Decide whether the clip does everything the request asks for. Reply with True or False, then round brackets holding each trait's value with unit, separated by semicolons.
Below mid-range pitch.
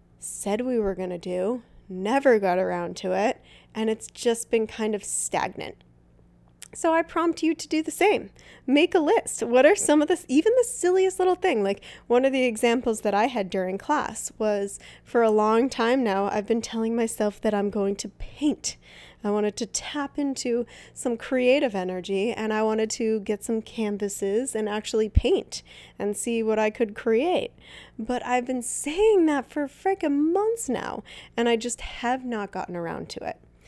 False (230 Hz)